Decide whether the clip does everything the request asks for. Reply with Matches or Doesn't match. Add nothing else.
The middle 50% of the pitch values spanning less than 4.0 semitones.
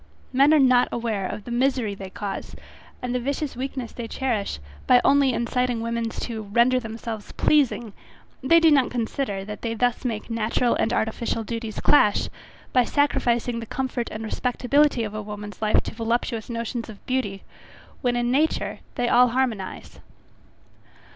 Matches